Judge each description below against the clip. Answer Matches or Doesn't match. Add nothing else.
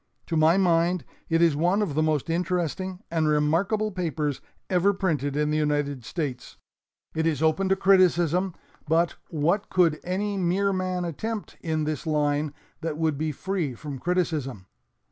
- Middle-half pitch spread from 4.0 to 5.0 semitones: Doesn't match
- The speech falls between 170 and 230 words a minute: Doesn't match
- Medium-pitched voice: Matches